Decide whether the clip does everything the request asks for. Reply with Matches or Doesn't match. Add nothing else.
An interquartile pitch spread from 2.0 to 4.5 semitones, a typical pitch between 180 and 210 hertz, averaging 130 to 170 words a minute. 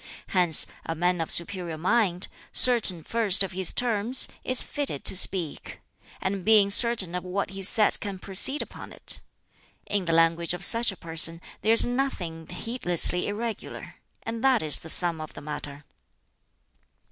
Doesn't match